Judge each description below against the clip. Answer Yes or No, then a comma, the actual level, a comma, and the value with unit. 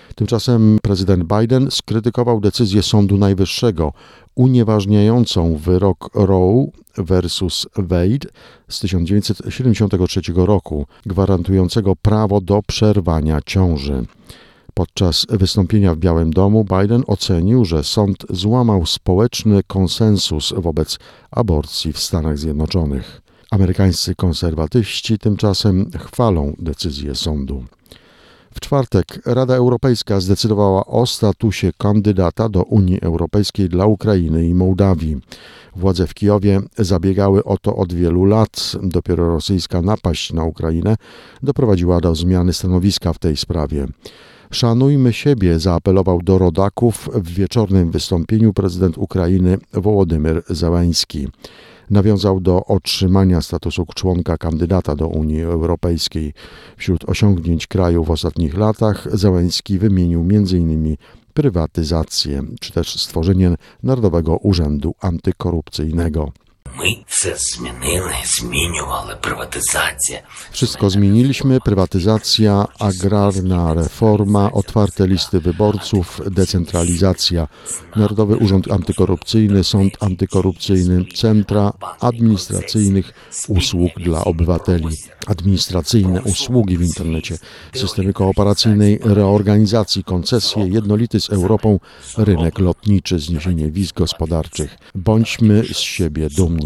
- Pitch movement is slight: No, average, 3.5 semitones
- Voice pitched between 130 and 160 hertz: No, very low, 95 Hz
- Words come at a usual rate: No, slow, 95 wpm